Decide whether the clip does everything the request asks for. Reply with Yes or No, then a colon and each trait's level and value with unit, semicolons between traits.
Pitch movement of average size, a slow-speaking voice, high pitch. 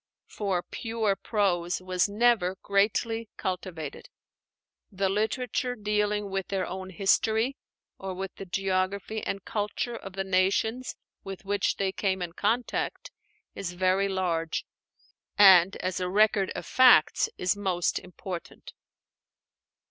No: narrow, 2.2 semitones; slow, 125 wpm; high, 195 Hz